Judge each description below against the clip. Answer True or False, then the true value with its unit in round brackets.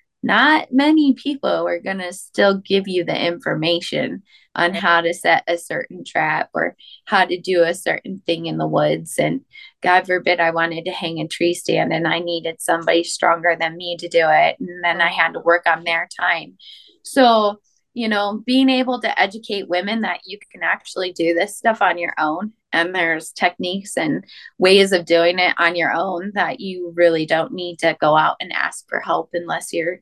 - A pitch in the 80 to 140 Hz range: False (175 Hz)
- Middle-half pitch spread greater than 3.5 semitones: False (2.9 semitones)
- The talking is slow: False (200 wpm)